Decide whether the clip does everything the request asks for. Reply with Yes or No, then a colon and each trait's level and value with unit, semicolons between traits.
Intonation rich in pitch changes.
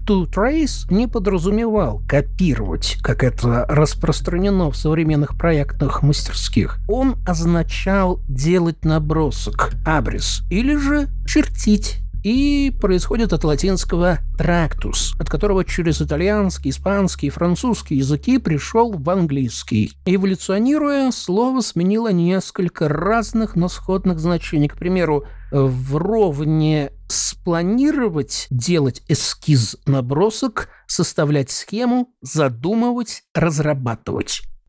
Yes: wide, 5.9 semitones